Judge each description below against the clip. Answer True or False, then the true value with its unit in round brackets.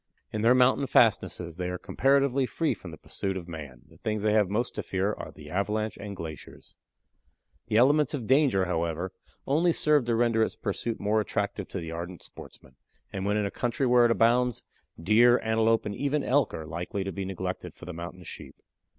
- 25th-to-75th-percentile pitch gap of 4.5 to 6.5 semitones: True (5.1 semitones)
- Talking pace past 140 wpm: True (200 wpm)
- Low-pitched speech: True (105 Hz)